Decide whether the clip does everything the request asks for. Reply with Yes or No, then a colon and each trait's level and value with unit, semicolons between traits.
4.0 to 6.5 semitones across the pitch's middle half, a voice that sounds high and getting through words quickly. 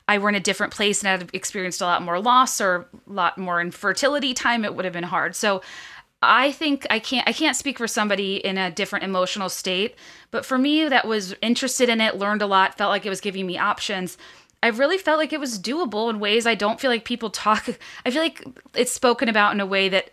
Yes: average, 4.3 semitones; high, 210 Hz; fast, 245 wpm